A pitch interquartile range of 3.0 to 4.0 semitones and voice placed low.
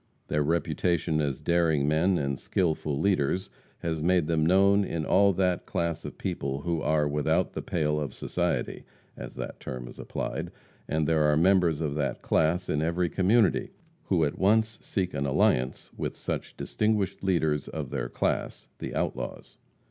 Yes: average, 3.5 semitones; very low, 80 Hz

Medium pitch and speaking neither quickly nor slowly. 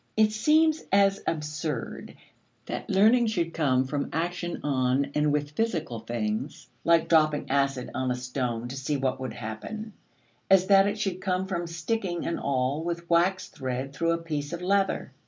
Yes: medium, 160 Hz; average, 170 wpm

